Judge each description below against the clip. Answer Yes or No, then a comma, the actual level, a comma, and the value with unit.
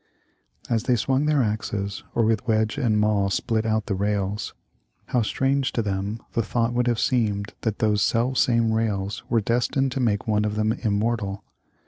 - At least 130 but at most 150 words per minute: No, average, 180 wpm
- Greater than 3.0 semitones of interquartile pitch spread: No, narrow, 2.4 semitones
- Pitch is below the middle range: Yes, low, 110 Hz